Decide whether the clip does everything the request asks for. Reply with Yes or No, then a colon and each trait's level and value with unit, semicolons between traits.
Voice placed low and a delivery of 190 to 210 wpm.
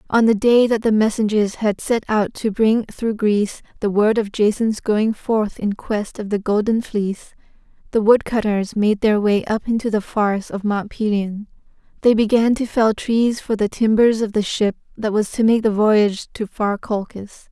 No: high, 215 Hz; average, 195 wpm